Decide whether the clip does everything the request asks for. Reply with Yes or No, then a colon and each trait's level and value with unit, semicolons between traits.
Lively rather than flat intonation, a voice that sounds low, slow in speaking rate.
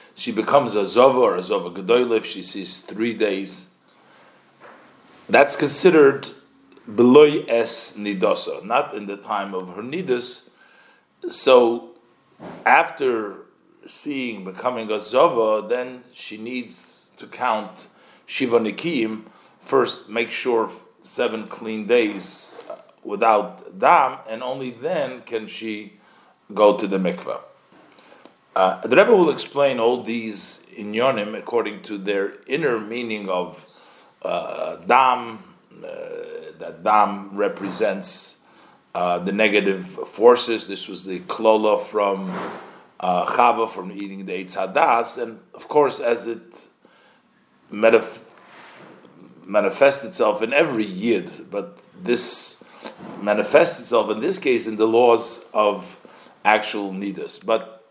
No: average, 3.4 semitones; low, 110 Hz; slow, 120 wpm